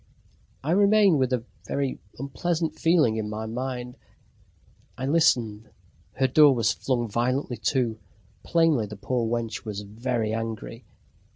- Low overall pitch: Yes, low, 125 Hz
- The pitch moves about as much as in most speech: Yes, average, 4.1 semitones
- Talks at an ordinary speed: No, slow, 130 wpm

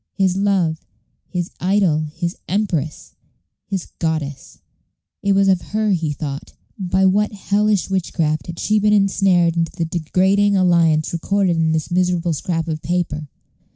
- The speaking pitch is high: No, medium, 175 Hz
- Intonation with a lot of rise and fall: No, average, 3.4 semitones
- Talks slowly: No, average, 145 wpm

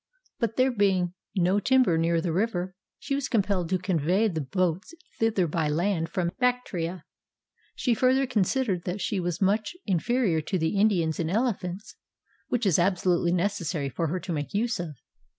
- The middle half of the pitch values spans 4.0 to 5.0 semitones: Yes, average, 4.3 semitones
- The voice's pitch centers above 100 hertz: Yes, medium, 185 Hz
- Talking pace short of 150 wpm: No, average, 175 wpm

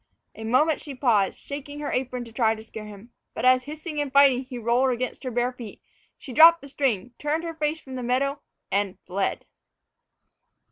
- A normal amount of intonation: Yes, average, 3.7 semitones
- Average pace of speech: Yes, average, 195 wpm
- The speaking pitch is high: Yes, very high, 255 Hz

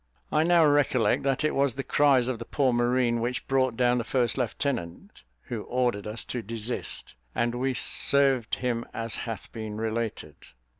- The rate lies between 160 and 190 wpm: Yes, average, 170 wpm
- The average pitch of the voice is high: No, low, 120 Hz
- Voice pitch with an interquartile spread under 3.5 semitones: Yes, narrow, 2.6 semitones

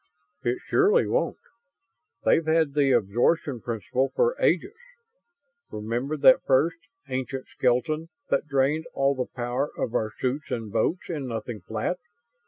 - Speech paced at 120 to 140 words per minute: Yes, slow, 135 wpm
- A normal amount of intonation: Yes, average, 4.6 semitones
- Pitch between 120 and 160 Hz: Yes, low, 135 Hz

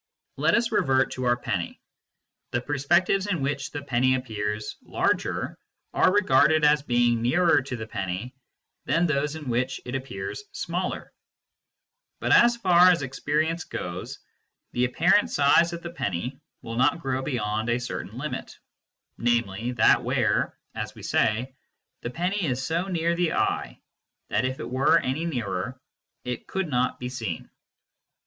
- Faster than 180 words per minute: No, average, 155 wpm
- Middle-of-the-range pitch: No, low, 130 Hz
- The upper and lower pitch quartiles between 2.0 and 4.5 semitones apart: No, average, 5.3 semitones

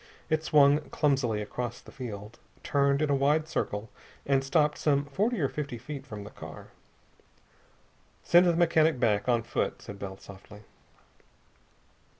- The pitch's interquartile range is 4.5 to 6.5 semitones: Yes, average, 5.3 semitones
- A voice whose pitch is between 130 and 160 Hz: Yes, medium, 140 Hz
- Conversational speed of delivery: Yes, average, 150 wpm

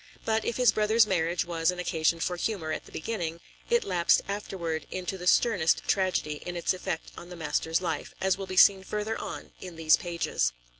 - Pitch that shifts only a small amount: No, average, 3.4 semitones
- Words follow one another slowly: No, average, 200 wpm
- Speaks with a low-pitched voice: No, medium, 180 Hz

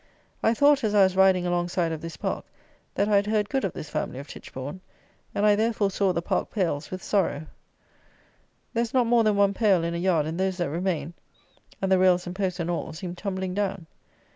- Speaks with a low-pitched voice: No, high, 190 Hz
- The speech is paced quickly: Yes, fast, 220 wpm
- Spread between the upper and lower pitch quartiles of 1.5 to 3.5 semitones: Yes, average, 2.9 semitones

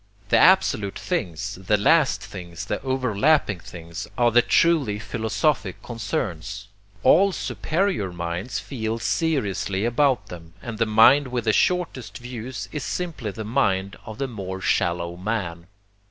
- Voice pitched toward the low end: Yes, low, 110 Hz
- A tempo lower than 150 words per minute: Yes, average, 140 wpm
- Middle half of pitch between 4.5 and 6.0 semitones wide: Yes, wide, 5.6 semitones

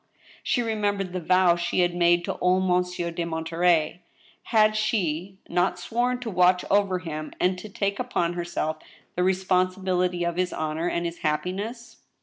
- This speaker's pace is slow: No, average, 160 wpm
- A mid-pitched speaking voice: Yes, medium, 180 Hz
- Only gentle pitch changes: Yes, narrow, 2.2 semitones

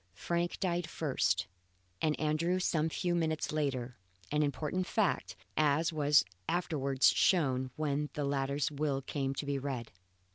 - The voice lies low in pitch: No, medium, 150 Hz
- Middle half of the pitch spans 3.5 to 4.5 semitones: No, average, 3.0 semitones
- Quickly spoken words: No, average, 140 wpm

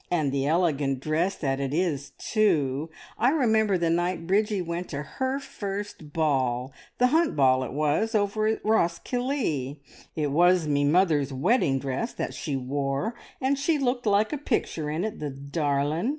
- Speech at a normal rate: Yes, average, 165 wpm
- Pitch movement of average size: No, wide, 7.3 semitones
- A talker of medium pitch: Yes, medium, 165 Hz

